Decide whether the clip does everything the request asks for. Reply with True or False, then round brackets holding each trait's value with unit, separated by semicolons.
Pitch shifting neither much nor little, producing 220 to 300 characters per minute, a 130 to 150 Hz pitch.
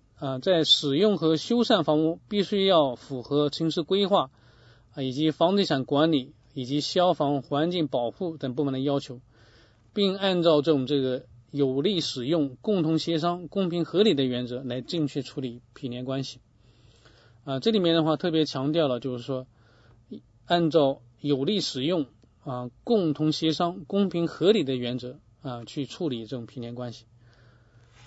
True (5.0 semitones; 240 characters per minute; 140 Hz)